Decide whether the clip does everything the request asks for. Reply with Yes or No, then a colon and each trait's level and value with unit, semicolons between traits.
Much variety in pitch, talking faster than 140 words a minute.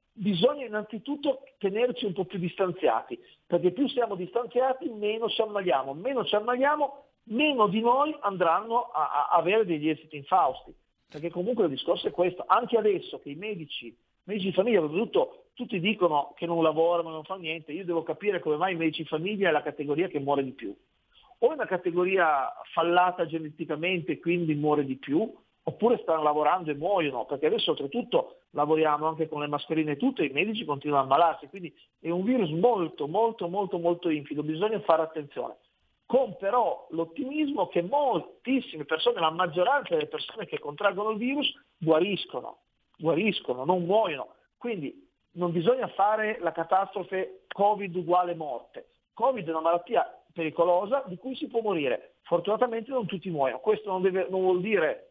Yes: wide, 6.7 semitones; fast, 170 wpm